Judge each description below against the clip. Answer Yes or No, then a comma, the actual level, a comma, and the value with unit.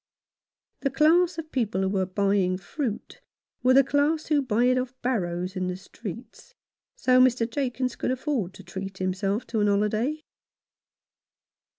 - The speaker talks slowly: No, average, 155 wpm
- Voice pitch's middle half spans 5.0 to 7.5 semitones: Yes, wide, 5.6 semitones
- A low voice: No, high, 235 Hz